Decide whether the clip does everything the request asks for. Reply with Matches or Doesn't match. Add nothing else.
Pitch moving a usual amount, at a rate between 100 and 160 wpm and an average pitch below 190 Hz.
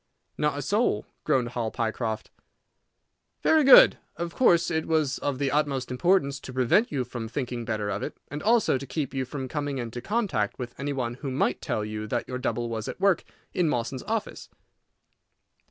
Doesn't match